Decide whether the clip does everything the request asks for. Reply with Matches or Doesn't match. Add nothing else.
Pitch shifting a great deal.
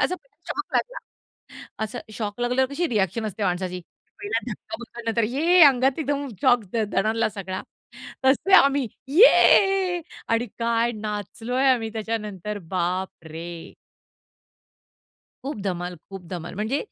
Matches